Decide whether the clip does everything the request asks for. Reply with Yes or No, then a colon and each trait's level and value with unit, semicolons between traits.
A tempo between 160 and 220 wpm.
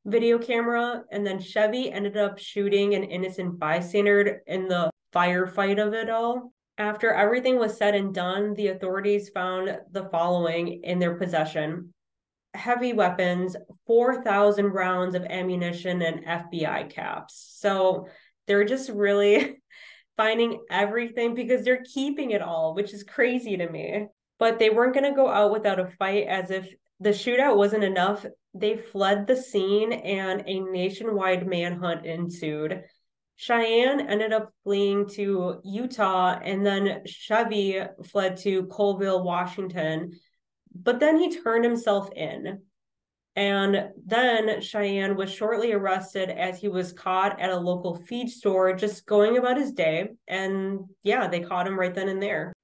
No: average, 145 wpm